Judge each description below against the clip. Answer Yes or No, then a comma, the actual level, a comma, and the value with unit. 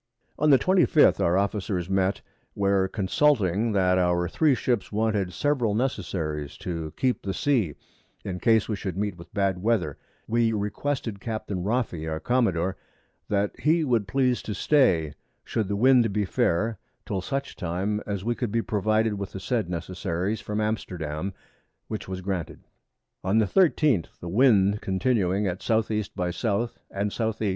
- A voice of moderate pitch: No, low, 100 Hz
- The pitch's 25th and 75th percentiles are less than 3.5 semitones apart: No, average, 3.8 semitones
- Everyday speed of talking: Yes, average, 165 wpm